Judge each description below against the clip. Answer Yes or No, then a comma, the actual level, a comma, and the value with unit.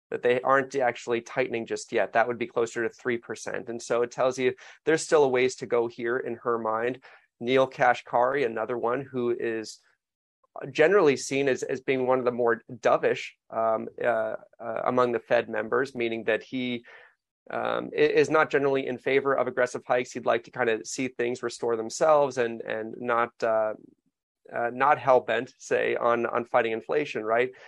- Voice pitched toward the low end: Yes, low, 120 Hz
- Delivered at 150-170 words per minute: No, average, 185 wpm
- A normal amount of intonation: No, narrow, 1.9 semitones